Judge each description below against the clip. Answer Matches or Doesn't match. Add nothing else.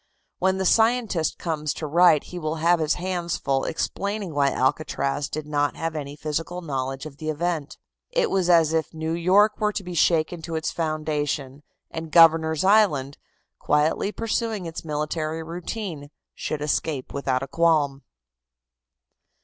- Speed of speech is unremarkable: Matches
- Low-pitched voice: Doesn't match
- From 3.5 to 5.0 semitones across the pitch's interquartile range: Doesn't match